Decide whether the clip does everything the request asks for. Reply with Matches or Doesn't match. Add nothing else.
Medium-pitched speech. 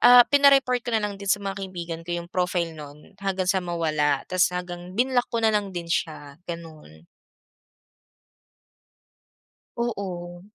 Matches